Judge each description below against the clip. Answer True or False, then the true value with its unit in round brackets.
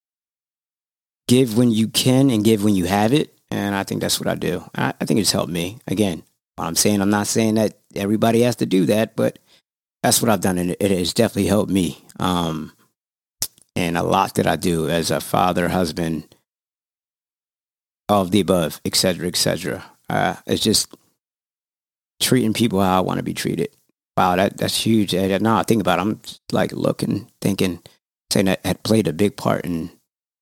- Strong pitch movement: False (3.7 semitones)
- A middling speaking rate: True (195 wpm)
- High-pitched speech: False (100 Hz)